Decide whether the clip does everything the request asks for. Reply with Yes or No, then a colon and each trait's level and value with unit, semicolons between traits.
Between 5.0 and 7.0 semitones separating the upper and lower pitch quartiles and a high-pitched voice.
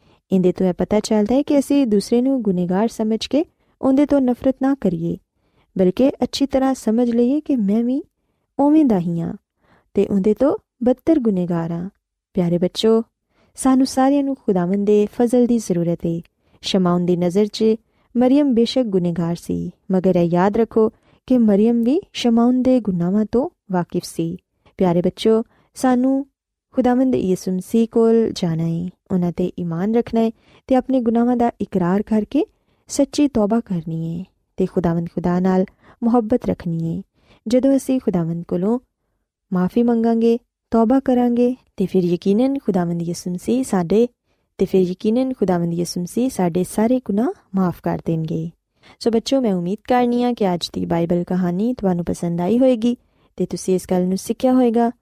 Yes: wide, 5.4 semitones; high, 215 Hz